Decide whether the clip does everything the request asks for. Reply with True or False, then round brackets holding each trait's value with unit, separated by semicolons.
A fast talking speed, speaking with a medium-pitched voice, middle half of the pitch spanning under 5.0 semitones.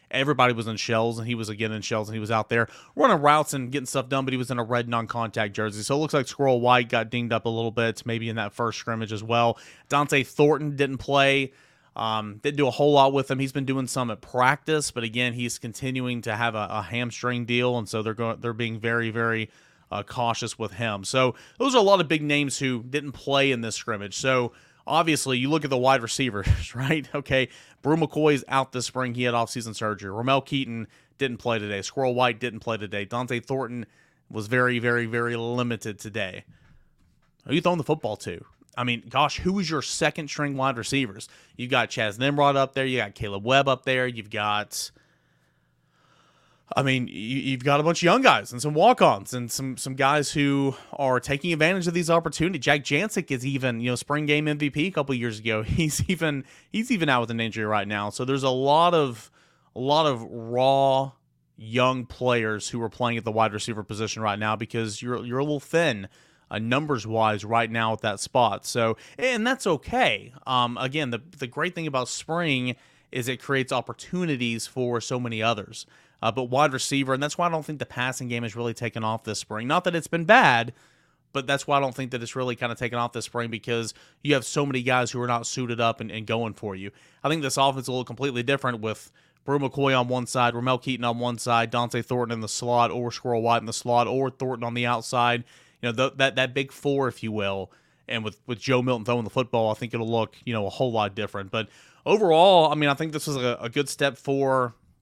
False (230 wpm; 125 Hz; 3.2 semitones)